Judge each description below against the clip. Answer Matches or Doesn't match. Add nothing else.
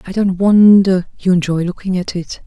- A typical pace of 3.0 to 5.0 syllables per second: Matches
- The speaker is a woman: Matches